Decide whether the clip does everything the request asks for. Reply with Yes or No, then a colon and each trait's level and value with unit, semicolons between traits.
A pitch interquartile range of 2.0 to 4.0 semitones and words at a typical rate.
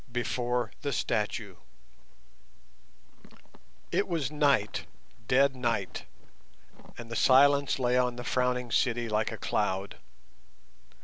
No: average, 3.0 semitones; slow, 90 wpm